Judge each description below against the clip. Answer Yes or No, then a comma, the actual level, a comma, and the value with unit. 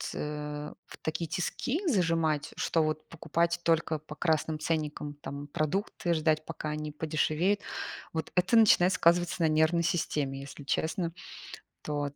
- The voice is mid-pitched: Yes, medium, 155 Hz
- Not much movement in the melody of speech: Yes, narrow, 2.2 semitones